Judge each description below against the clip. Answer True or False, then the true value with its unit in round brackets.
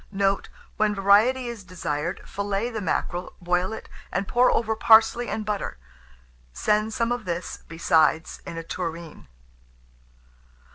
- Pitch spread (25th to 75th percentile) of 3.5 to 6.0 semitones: True (4.0 semitones)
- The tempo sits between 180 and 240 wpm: False (135 wpm)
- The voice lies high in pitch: True (200 Hz)